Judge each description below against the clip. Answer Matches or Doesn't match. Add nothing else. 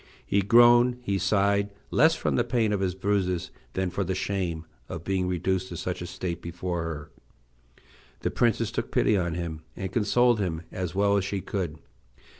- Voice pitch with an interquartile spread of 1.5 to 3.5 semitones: Matches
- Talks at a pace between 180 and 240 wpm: Matches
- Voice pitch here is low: Matches